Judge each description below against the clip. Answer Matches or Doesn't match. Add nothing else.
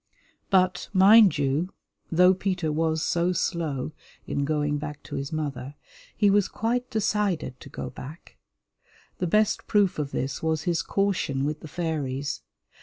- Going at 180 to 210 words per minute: Doesn't match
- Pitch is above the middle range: Doesn't match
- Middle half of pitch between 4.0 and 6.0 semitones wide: Matches